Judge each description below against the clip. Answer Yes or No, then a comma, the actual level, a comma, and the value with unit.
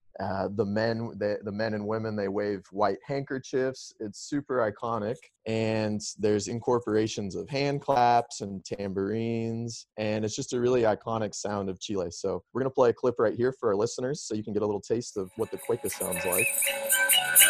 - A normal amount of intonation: Yes, average, 4.0 semitones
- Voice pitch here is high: No, low, 110 Hz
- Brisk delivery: No, average, 195 wpm